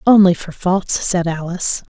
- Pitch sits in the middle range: Yes, medium, 180 Hz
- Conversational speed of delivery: Yes, average, 155 wpm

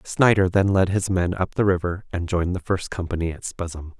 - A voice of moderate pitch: No, very low, 90 Hz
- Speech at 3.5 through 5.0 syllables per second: No, 5.5 syllables/s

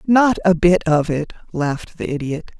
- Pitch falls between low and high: Yes, medium, 170 Hz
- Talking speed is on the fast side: No, average, 185 wpm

